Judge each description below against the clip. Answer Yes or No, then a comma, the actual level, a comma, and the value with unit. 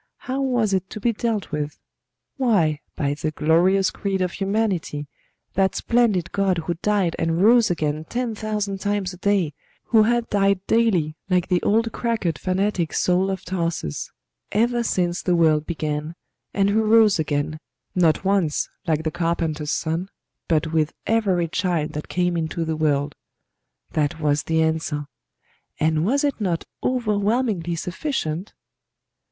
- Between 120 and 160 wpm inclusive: Yes, average, 150 wpm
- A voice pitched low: No, medium, 180 Hz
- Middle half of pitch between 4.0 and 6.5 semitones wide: Yes, average, 4.7 semitones